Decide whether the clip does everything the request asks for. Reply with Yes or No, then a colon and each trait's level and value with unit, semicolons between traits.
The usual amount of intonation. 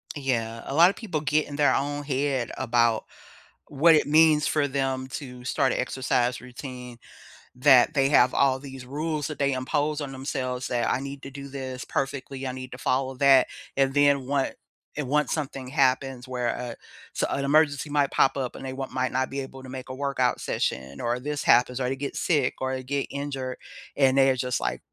No: narrow, 1.9 semitones